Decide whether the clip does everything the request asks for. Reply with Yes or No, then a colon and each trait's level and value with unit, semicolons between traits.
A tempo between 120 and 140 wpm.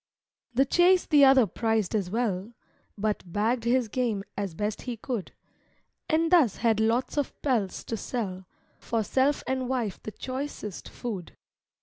No: average, 150 wpm